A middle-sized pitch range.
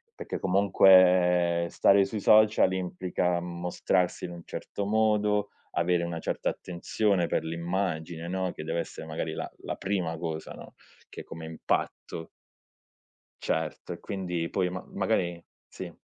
No: narrow, 2.1 semitones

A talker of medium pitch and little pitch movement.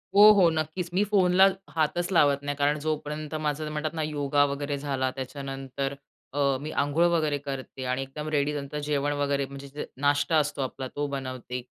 Yes: medium, 145 Hz; narrow, 1.9 semitones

